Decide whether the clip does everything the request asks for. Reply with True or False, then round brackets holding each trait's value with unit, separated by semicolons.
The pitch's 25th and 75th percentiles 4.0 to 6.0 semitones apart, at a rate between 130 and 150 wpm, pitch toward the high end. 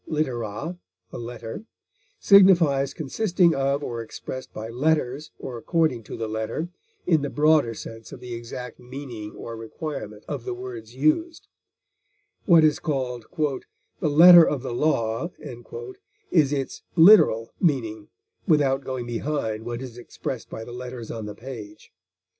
False (4.9 semitones; 140 wpm; 130 Hz)